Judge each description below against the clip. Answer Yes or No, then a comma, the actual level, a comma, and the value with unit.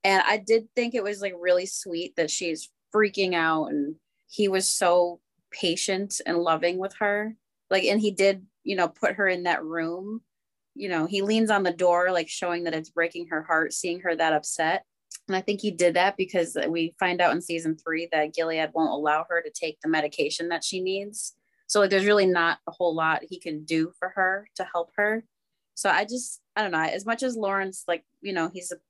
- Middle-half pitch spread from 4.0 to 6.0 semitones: No, average, 3.2 semitones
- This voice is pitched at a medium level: Yes, medium, 180 Hz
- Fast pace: Yes, fast, 220 wpm